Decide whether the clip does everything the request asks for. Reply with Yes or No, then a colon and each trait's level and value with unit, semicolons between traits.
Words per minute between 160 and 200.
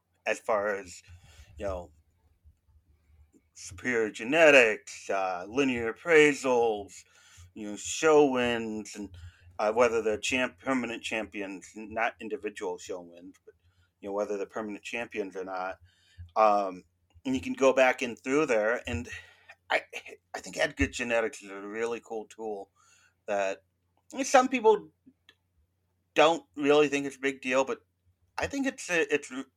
No: average, 150 wpm